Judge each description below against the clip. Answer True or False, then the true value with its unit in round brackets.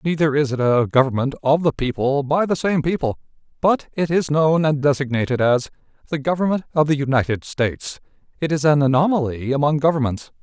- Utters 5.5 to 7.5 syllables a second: True (5.8 syllables/s)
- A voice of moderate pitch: True (145 Hz)